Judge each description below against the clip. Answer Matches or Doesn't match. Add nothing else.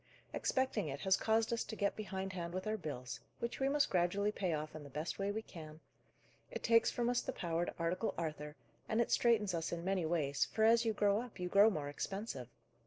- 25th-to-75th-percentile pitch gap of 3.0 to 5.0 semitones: Doesn't match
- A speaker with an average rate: Doesn't match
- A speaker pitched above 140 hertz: Matches